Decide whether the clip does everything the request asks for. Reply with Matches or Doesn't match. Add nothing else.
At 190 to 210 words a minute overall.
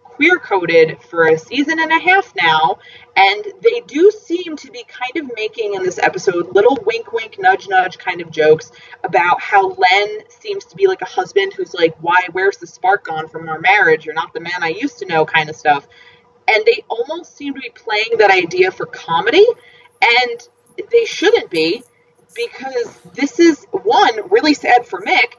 Matches